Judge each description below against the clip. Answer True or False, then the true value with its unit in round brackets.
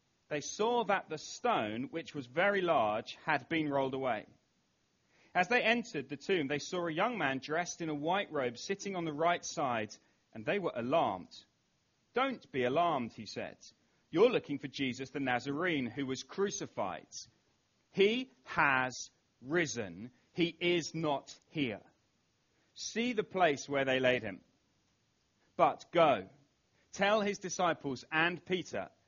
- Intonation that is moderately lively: False (5.8 semitones)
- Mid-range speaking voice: True (160 Hz)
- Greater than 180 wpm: False (150 wpm)